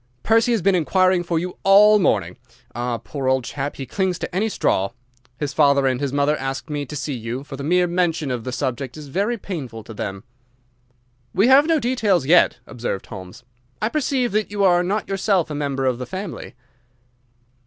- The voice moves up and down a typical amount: No, wide, 6.8 semitones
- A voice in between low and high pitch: Yes, medium, 155 Hz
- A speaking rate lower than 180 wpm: No, average, 200 wpm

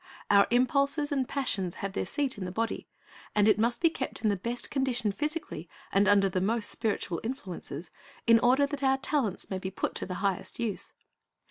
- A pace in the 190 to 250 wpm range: Yes, average, 200 wpm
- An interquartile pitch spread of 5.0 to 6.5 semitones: Yes, average, 5.3 semitones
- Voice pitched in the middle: No, high, 225 Hz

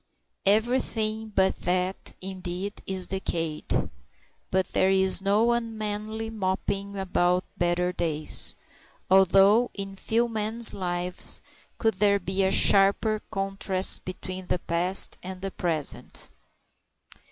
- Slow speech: Yes, slow, 110 wpm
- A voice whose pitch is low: No, high, 195 Hz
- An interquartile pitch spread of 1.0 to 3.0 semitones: Yes, narrow, 2.6 semitones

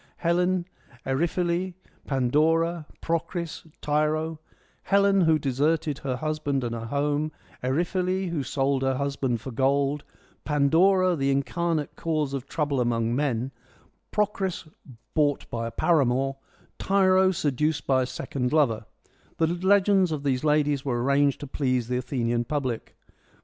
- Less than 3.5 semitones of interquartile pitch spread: No, average, 4.1 semitones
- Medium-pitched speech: Yes, medium, 145 Hz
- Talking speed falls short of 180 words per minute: Yes, slow, 135 wpm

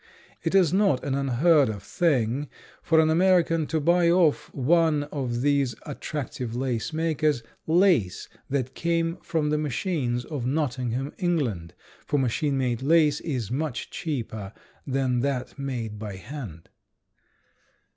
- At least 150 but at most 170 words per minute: No, slow, 135 wpm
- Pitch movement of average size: Yes, average, 4.6 semitones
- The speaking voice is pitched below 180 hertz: Yes, medium, 140 Hz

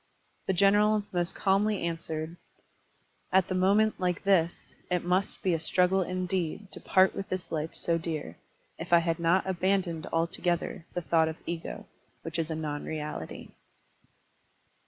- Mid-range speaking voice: Yes, medium, 175 Hz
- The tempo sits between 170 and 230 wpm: No, average, 155 wpm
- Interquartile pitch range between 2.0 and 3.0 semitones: Yes, narrow, 2.5 semitones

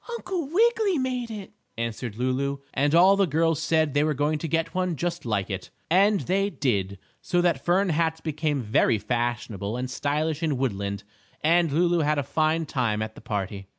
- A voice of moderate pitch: Yes, medium, 150 Hz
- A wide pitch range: Yes, wide, 6.4 semitones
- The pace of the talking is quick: No, average, 185 wpm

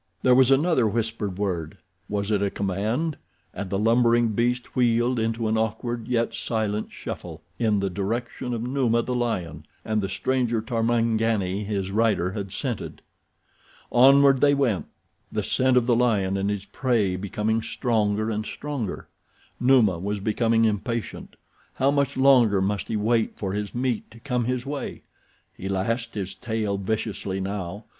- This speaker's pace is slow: No, average, 150 wpm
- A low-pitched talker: Yes, low, 110 Hz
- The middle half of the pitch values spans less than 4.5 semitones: Yes, average, 3.3 semitones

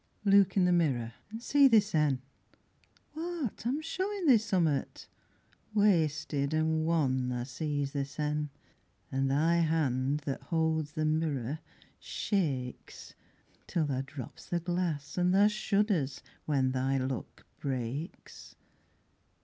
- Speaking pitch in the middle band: Yes, medium, 155 Hz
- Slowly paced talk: Yes, slow, 125 wpm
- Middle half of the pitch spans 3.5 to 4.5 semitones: No, wide, 5.4 semitones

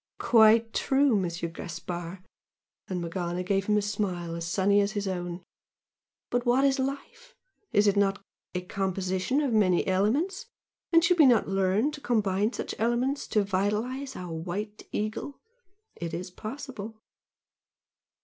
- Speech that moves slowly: No, average, 145 wpm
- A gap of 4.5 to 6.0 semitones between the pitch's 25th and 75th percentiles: Yes, average, 5.0 semitones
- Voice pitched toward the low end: No, high, 205 Hz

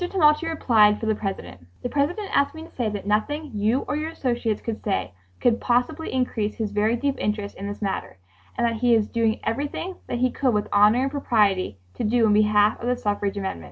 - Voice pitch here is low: No, high, 225 Hz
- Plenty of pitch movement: No, average, 4.2 semitones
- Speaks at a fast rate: Yes, fast, 215 wpm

